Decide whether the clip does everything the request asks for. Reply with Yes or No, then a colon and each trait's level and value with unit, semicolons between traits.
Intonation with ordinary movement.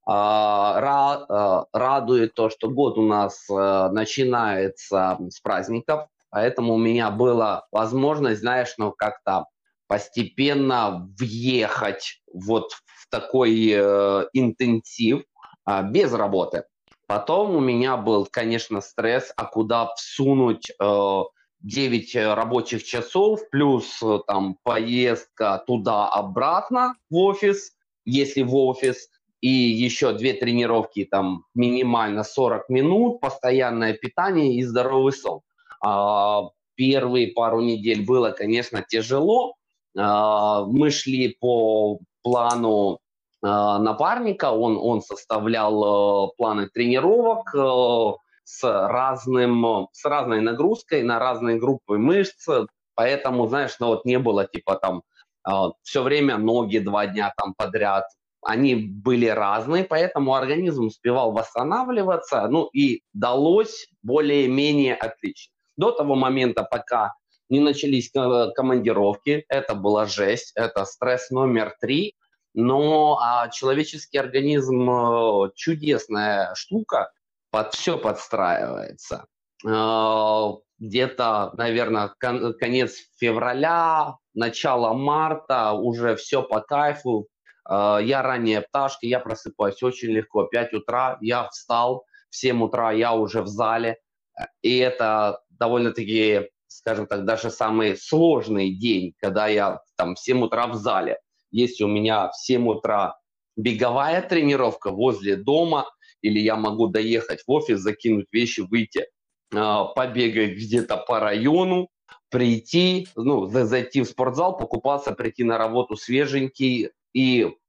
Yes: average, 3.6 semitones